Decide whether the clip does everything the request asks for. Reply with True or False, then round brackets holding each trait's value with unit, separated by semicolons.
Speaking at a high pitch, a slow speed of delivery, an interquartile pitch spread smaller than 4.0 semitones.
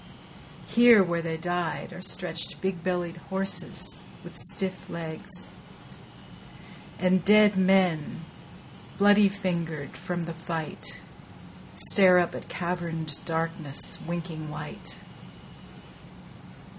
False (175 Hz; 95 wpm; 2.5 semitones)